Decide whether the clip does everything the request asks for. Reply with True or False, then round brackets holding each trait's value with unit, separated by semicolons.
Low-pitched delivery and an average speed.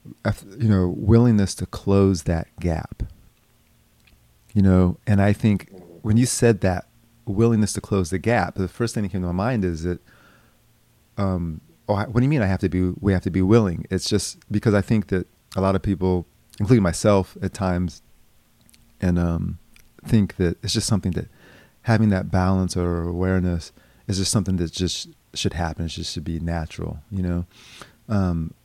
True (95 Hz; 185 wpm)